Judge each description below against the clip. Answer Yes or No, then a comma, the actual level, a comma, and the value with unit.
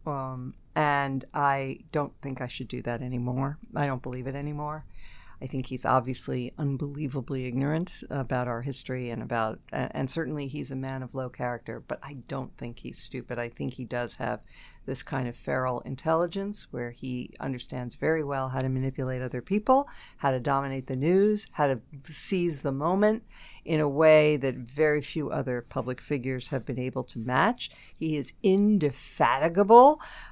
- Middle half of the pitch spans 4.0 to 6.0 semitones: No, average, 2.9 semitones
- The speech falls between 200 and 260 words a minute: No, average, 170 wpm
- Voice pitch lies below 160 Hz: Yes, low, 135 Hz